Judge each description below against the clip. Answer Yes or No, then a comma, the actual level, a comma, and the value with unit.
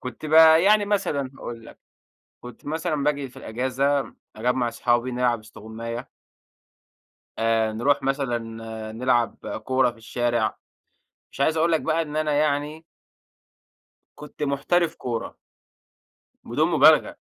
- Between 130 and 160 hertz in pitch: Yes, low, 135 Hz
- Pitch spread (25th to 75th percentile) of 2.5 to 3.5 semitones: No, average, 4.3 semitones